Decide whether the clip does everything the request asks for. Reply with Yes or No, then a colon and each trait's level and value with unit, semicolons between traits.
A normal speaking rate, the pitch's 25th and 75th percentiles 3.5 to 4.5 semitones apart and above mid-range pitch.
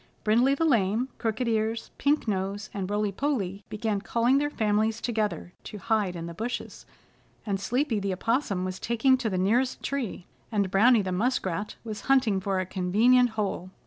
Yes: average, 175 wpm; average, 3.9 semitones; high, 215 Hz